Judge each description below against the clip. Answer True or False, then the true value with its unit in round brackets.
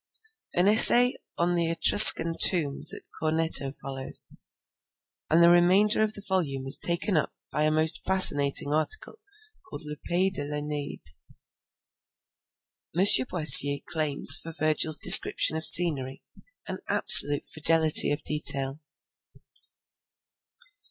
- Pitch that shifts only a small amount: False (3.2 semitones)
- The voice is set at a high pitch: False (155 Hz)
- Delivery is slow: True (120 wpm)